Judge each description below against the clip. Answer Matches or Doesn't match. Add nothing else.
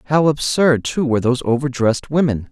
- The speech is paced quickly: Doesn't match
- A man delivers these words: Matches